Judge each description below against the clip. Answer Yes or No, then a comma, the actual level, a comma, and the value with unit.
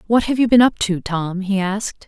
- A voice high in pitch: Yes, high, 205 Hz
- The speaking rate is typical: No, fast, 260 wpm